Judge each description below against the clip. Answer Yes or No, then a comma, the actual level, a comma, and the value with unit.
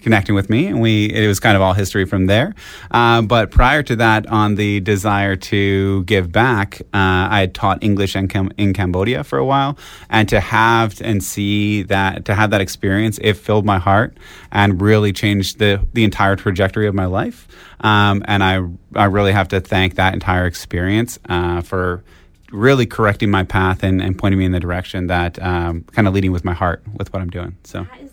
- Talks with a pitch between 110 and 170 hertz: No, low, 100 Hz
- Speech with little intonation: Yes, narrow, 2.2 semitones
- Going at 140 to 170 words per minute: No, fast, 205 wpm